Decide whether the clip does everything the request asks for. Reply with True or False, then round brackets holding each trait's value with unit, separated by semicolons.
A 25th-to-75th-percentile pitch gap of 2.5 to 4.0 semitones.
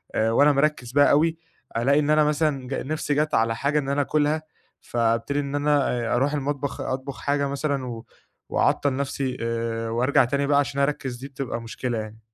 True (3.1 semitones)